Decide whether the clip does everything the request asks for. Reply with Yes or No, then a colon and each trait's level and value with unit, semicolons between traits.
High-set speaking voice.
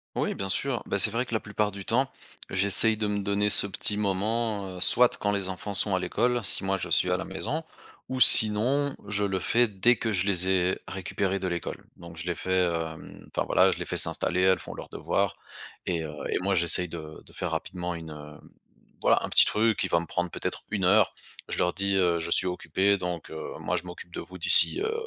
No: very low, 95 Hz